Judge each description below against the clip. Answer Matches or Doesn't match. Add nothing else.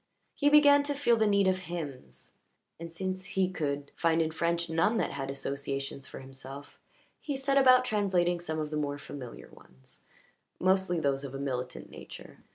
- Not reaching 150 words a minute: Doesn't match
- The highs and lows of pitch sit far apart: Matches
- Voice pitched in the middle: Matches